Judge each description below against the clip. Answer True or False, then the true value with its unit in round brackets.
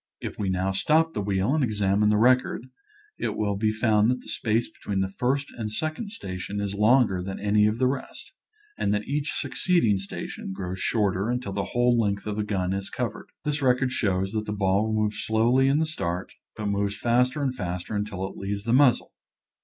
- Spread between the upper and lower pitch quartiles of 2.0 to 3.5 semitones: False (4.2 semitones)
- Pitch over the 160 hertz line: False (105 Hz)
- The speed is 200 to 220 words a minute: True (205 wpm)